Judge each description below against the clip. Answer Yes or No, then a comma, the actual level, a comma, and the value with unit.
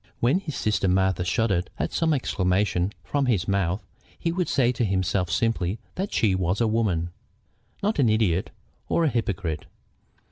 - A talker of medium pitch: No, low, 105 Hz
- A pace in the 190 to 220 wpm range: No, average, 165 wpm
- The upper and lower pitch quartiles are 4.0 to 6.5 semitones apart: Yes, average, 5.0 semitones